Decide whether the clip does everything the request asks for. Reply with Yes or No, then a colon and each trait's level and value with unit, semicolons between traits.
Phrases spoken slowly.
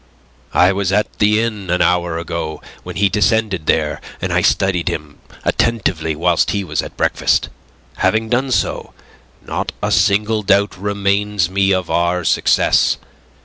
No: average, 150 wpm